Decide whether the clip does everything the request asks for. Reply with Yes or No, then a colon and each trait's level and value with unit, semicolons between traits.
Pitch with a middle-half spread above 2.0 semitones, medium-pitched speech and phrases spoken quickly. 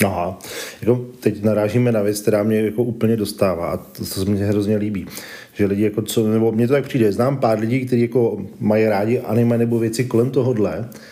No: narrow, 2.4 semitones; low, 110 Hz; fast, 205 wpm